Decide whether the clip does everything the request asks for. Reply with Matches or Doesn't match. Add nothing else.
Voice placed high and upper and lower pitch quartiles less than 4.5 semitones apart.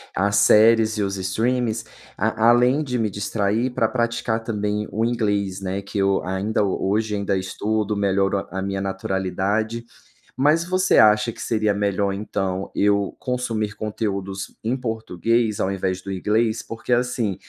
Doesn't match